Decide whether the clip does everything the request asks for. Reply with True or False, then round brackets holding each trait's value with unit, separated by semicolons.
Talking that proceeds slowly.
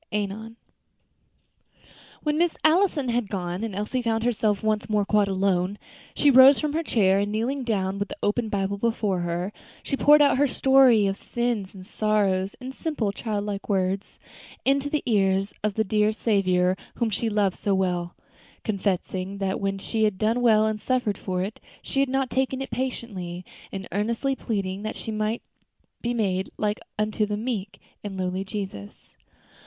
False (175 wpm)